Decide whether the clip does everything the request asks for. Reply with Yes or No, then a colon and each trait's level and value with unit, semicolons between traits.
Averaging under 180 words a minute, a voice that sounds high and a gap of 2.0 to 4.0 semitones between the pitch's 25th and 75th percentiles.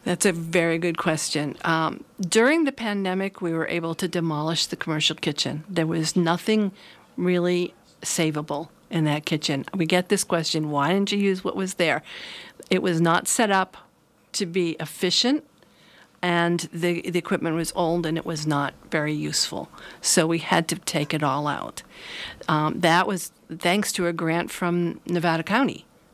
No: average, 170 wpm; medium, 170 Hz; narrow, 2.4 semitones